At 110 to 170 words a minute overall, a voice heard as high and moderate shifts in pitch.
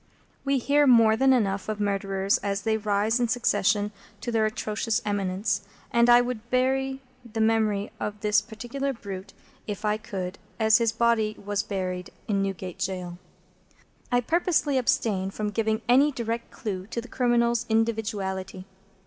Yes: average, 155 wpm; high, 220 Hz; average, 3.0 semitones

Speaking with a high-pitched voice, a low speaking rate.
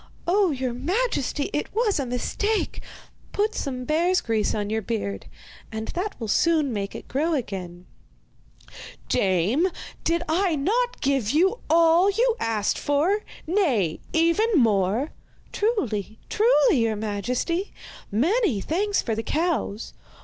Yes: very high, 295 Hz; slow, 130 wpm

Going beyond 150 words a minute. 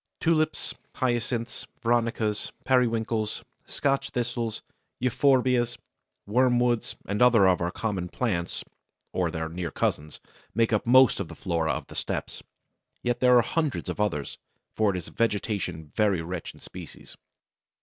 No: average, 145 wpm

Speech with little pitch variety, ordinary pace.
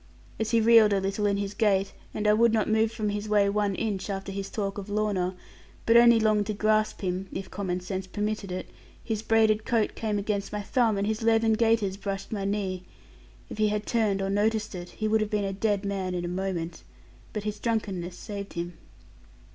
No: narrow, 1.9 semitones; fast, 215 wpm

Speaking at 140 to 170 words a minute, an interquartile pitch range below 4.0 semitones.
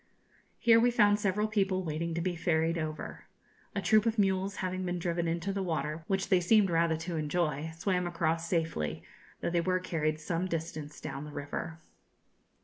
No: average, 180 wpm; average, 2.9 semitones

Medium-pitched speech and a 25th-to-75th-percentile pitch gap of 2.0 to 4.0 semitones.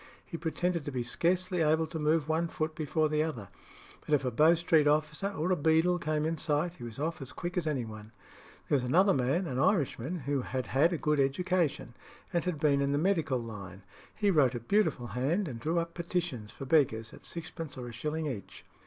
No: medium, 155 Hz; average, 4.4 semitones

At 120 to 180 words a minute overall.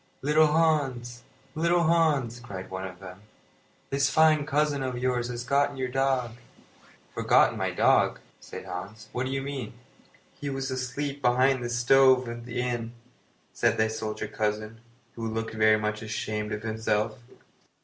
Yes: average, 155 wpm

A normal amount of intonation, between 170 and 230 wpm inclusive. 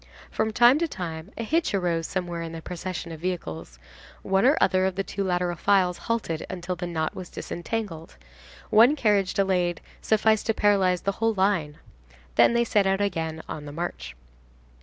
Yes: average, 3.5 semitones; average, 180 wpm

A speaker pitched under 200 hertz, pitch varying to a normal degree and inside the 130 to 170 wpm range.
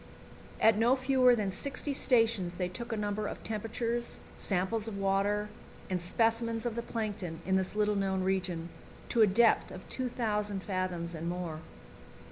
No: high, 210 Hz; average, 3.5 semitones; average, 160 wpm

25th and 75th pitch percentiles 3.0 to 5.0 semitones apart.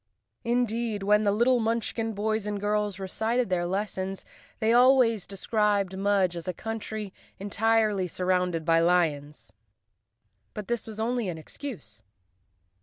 Yes: average, 3.4 semitones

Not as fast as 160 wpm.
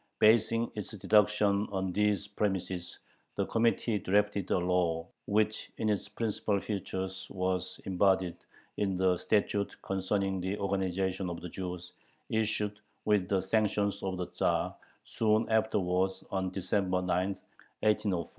Yes: slow, 135 wpm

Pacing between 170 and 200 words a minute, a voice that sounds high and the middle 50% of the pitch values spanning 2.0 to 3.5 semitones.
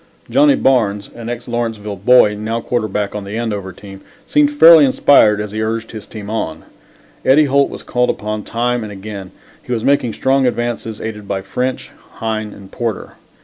No: average, 180 wpm; low, 110 Hz; average, 3.0 semitones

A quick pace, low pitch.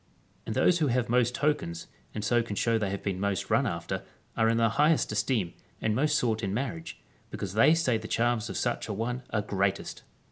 Yes: fast, 215 wpm; low, 110 Hz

